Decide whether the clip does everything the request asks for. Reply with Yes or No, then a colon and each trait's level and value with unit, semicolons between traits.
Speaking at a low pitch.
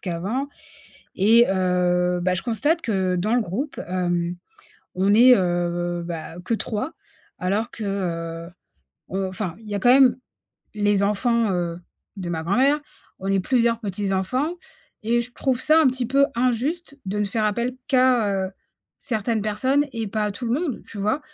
No: high, 210 Hz